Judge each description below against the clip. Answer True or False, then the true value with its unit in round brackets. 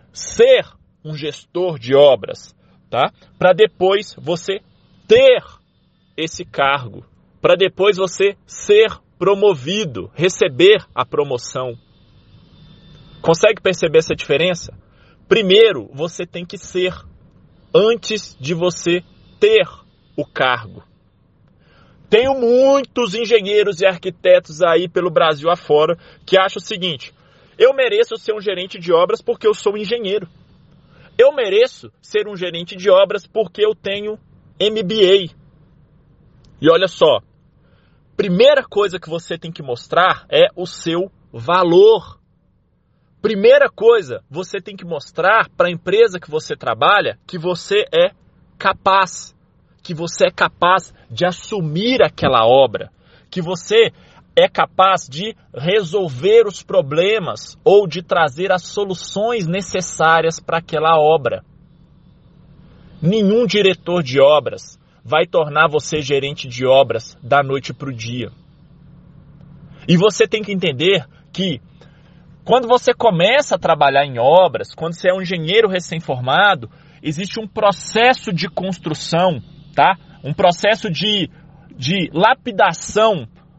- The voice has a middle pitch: True (180 Hz)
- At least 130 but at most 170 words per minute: False (120 wpm)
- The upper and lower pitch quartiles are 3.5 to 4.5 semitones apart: False (5.1 semitones)